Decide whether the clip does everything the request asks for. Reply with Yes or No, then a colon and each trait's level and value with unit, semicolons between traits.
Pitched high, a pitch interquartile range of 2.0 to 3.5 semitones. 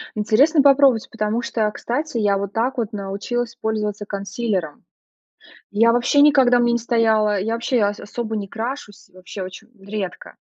Yes: high, 220 Hz; average, 2.9 semitones